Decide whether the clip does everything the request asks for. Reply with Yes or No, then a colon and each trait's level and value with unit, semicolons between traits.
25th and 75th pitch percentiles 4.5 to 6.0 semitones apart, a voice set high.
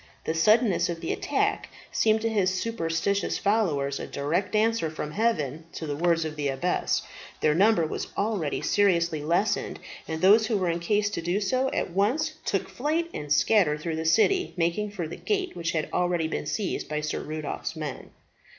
No: average, 5.2 semitones; medium, 175 Hz